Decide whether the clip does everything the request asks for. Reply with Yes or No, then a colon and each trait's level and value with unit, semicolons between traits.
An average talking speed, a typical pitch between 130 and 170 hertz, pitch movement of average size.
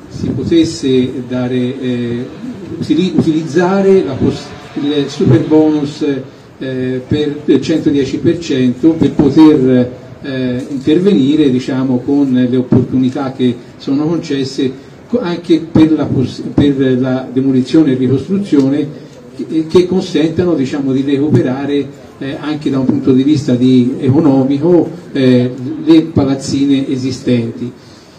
No: slow, 110 wpm; medium, 140 Hz; average, 3.3 semitones